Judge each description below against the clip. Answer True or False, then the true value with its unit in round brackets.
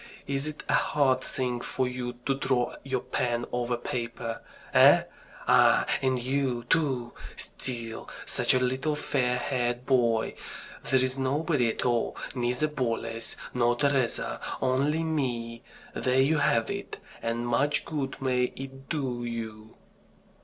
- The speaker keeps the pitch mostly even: True (2.1 semitones)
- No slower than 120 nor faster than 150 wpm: True (135 wpm)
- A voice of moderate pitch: False (125 Hz)